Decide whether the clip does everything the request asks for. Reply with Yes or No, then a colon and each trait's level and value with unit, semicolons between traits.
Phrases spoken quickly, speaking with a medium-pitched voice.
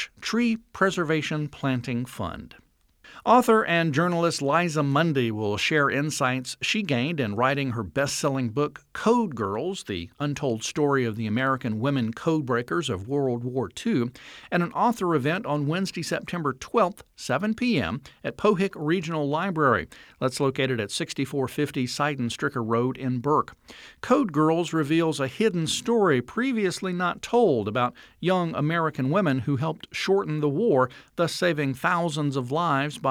No: average, 145 wpm; medium, 150 Hz